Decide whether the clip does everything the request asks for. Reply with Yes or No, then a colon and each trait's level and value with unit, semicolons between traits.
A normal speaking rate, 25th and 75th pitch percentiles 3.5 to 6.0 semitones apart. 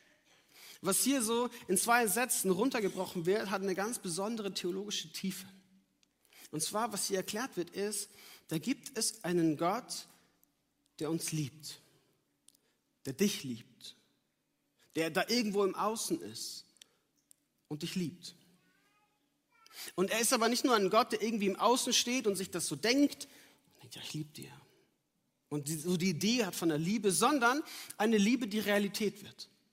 Yes: average, 160 wpm; average, 4.5 semitones